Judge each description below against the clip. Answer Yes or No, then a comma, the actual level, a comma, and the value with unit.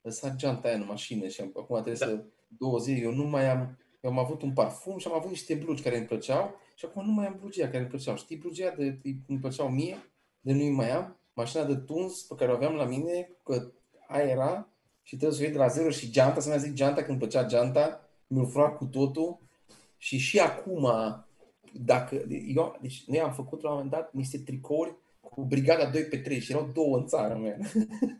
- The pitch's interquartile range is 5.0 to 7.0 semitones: No, average, 3.5 semitones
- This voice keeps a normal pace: No, fast, 225 wpm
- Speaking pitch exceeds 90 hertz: Yes, medium, 140 Hz